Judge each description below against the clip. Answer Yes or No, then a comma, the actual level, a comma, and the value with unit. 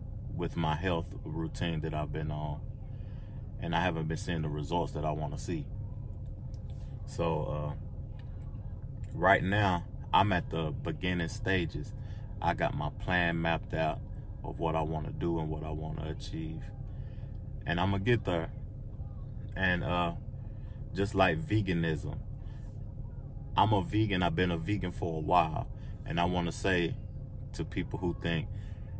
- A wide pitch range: No, average, 4.8 semitones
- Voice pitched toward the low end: Yes, very low, 95 Hz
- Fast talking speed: No, average, 155 wpm